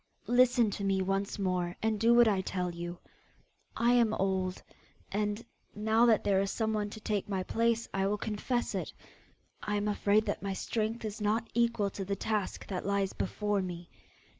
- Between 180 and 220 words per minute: Yes, average, 185 wpm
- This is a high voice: Yes, high, 205 Hz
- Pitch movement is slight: Yes, narrow, 2.3 semitones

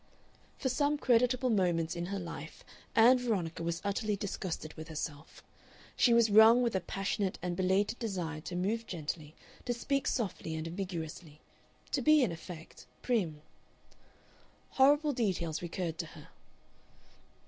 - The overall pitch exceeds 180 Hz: Yes, high, 190 Hz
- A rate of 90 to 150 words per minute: Yes, average, 140 wpm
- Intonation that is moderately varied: No, wide, 6.0 semitones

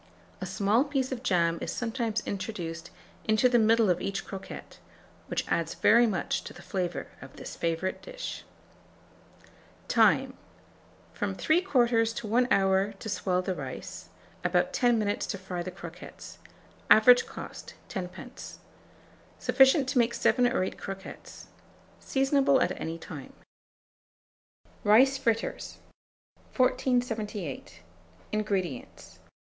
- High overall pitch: Yes, high, 215 Hz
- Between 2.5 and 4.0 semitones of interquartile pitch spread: No, average, 5.0 semitones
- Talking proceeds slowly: Yes, slow, 120 wpm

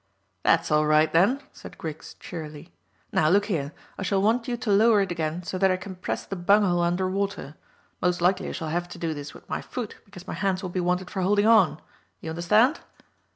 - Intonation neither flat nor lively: Yes, average, 3.3 semitones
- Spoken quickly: Yes, fast, 225 wpm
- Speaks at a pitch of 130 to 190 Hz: Yes, medium, 185 Hz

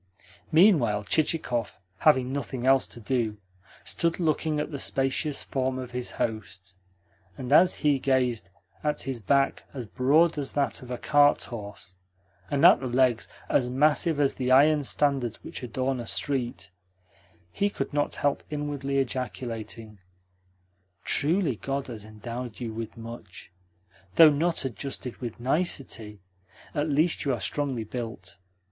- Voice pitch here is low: Yes, low, 130 Hz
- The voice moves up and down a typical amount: Yes, average, 3.8 semitones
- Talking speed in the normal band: Yes, average, 145 wpm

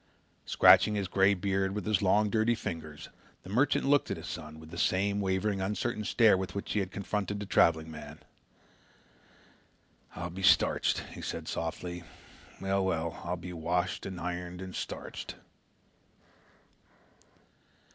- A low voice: Yes, very low, 95 Hz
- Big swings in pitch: No, average, 2.8 semitones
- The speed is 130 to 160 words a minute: Yes, average, 145 wpm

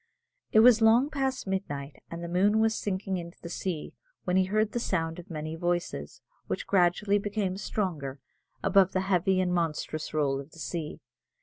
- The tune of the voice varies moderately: Yes, average, 4.0 semitones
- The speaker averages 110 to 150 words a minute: No, average, 180 wpm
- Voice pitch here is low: No, medium, 185 Hz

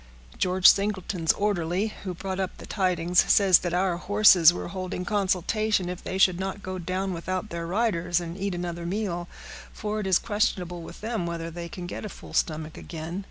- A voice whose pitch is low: No, medium, 185 Hz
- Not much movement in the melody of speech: Yes, narrow, 2.3 semitones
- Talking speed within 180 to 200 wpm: Yes, average, 190 wpm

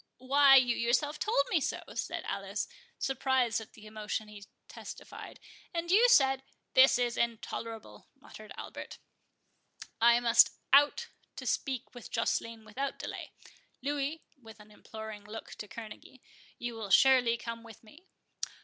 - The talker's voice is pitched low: No, high, 240 Hz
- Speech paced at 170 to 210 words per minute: No, average, 140 wpm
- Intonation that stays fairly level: No, average, 3.5 semitones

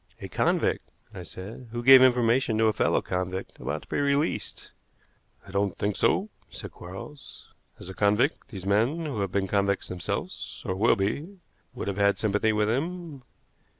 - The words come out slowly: No, average, 175 wpm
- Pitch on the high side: No, low, 105 Hz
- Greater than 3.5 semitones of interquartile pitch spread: Yes, average, 5.2 semitones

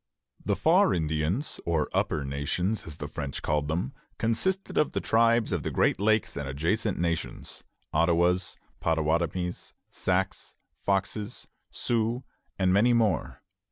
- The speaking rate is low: Yes, slow, 130 wpm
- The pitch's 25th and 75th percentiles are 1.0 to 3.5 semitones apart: No, wide, 5.6 semitones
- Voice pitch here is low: Yes, very low, 90 Hz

